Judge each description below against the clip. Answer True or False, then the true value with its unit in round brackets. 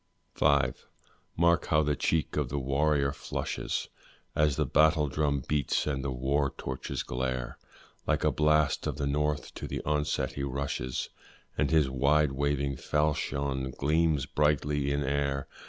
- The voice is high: False (70 Hz)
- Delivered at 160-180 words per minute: False (150 wpm)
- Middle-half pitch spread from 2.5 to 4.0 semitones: False (1.7 semitones)